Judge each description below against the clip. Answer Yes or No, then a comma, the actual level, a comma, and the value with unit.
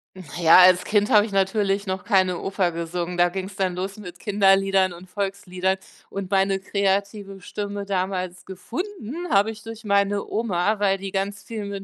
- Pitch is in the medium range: No, high, 195 Hz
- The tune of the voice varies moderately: No, narrow, 1.6 semitones